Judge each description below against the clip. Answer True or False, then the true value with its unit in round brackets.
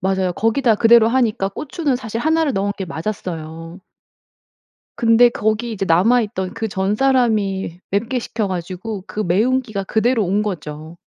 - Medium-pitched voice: False (210 Hz)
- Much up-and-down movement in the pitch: False (3.9 semitones)